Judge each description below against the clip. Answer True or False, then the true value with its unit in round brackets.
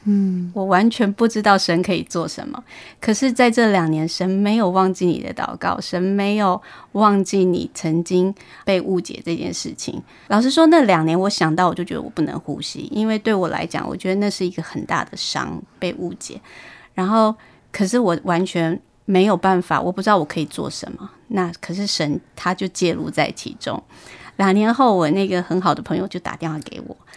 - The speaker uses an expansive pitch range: False (3.1 semitones)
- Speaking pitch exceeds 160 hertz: True (190 Hz)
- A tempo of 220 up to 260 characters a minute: False (285 characters per minute)